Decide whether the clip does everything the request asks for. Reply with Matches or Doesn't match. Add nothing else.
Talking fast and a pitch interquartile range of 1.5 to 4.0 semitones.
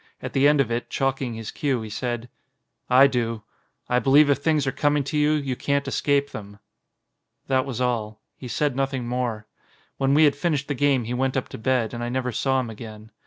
Matches